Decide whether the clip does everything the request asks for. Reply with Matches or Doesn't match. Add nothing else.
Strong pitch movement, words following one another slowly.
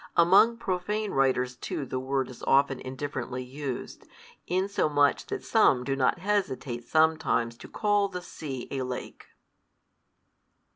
Matches